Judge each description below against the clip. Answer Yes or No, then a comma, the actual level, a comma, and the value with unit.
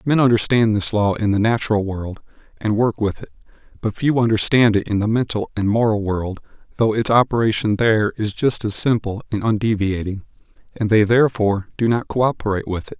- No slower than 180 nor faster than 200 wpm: Yes, average, 185 wpm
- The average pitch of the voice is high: No, low, 110 Hz